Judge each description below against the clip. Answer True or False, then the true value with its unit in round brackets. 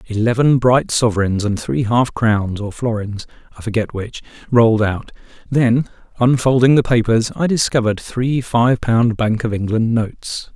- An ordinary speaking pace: True (155 wpm)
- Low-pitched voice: True (115 Hz)